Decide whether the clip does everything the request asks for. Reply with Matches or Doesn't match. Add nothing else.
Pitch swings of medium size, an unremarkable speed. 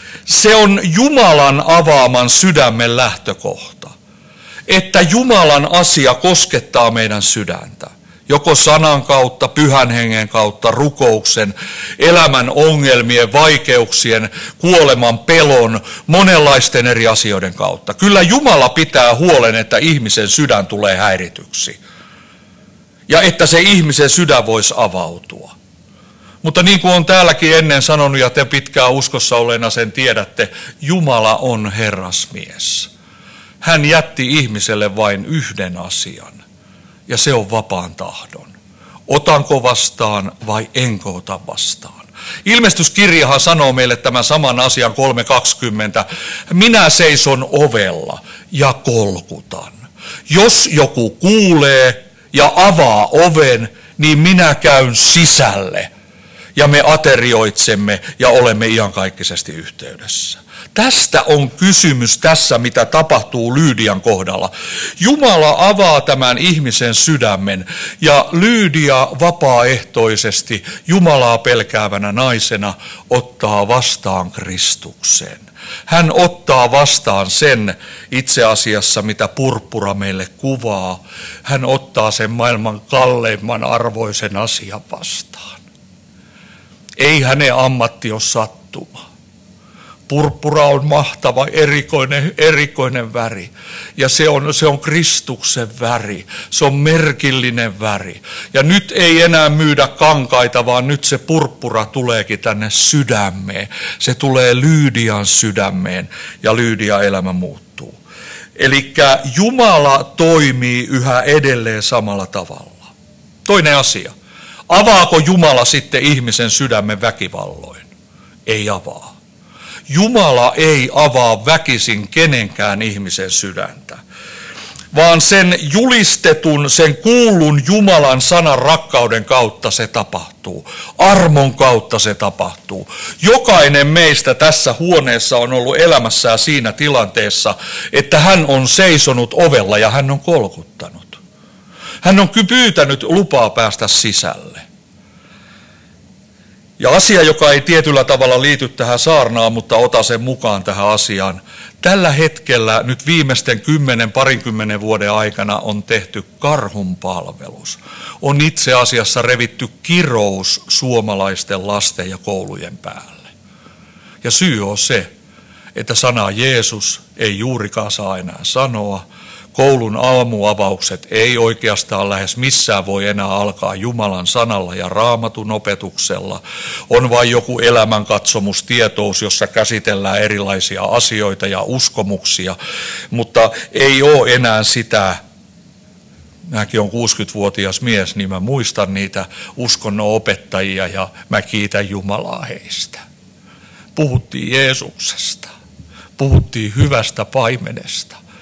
Doesn't match